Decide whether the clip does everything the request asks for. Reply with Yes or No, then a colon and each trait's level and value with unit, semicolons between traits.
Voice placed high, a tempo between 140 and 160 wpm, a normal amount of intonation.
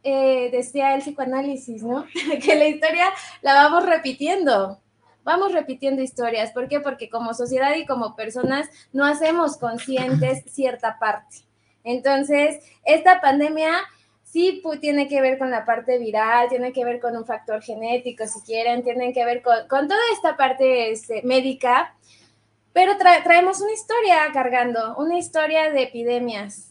Yes: very high, 265 Hz; average, 155 wpm; average, 4.4 semitones